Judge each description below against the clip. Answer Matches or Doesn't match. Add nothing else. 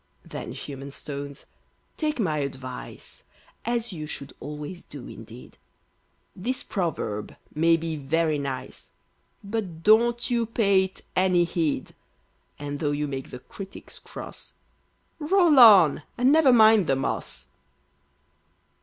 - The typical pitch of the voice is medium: Matches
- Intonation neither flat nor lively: Doesn't match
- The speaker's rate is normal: Doesn't match